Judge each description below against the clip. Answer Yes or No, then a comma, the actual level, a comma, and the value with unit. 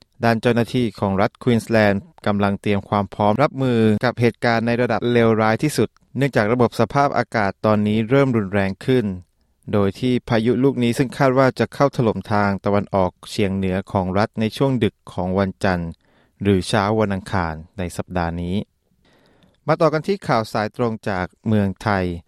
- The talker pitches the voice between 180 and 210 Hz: No, low, 110 Hz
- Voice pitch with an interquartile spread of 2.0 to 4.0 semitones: Yes, average, 3.5 semitones